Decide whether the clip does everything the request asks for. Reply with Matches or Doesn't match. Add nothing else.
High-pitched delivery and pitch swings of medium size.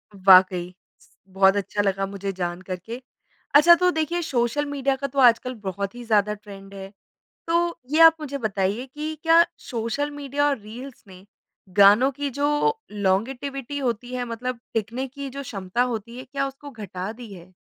Doesn't match